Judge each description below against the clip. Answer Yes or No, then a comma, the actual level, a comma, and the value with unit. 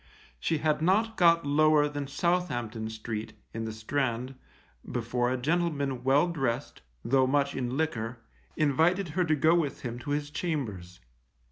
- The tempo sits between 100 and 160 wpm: Yes, average, 150 wpm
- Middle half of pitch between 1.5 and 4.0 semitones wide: No, average, 4.7 semitones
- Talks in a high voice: No, medium, 140 Hz